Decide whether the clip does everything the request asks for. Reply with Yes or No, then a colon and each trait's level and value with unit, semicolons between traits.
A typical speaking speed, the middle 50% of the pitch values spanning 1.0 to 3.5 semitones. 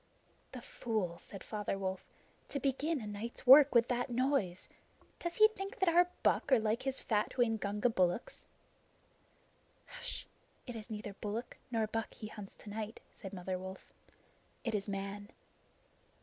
No: average, 155 wpm; average, 4.2 semitones